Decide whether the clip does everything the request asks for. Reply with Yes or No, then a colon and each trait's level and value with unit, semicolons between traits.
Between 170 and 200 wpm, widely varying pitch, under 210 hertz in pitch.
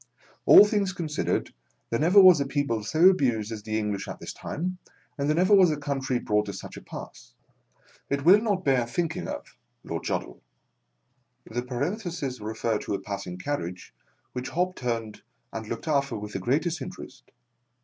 Yes: average, 180 wpm; wide, 7.8 semitones; medium, 140 Hz